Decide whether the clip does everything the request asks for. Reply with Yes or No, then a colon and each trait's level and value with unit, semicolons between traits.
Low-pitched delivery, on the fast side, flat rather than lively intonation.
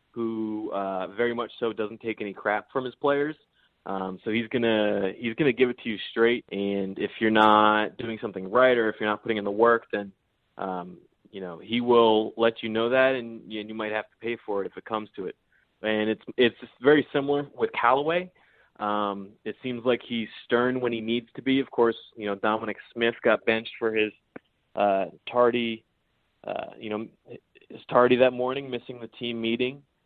Yes: low, 115 Hz; fast, 210 wpm; narrow, 2.3 semitones